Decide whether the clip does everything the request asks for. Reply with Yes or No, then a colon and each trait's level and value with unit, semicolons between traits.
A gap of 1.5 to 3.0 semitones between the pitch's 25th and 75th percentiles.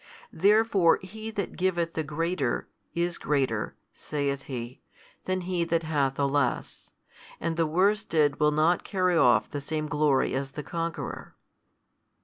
No: average, 3.9 semitones